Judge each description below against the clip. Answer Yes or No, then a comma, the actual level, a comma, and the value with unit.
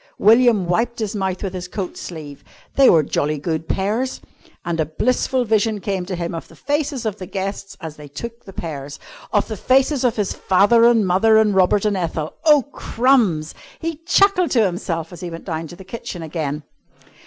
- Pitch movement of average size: No, wide, 5.7 semitones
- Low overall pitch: No, high, 195 Hz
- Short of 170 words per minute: No, average, 200 wpm